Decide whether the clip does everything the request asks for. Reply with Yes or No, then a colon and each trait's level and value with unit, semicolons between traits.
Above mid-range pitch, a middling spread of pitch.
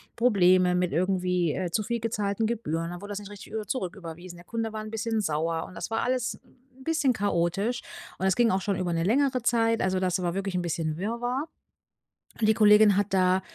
Yes: high, 200 Hz; average, 4.1 semitones